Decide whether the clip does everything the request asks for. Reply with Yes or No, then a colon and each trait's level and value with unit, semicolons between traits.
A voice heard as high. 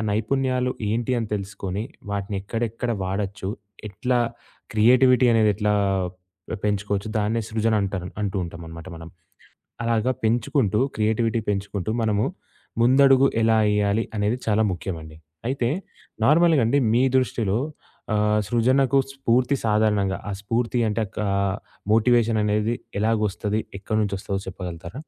No: low, 110 Hz